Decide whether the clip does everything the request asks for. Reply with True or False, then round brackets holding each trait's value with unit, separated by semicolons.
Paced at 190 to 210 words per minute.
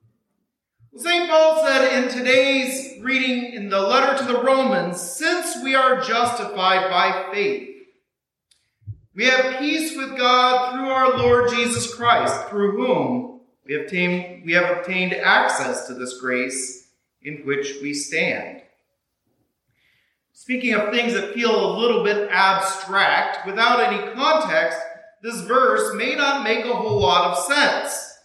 False (140 wpm)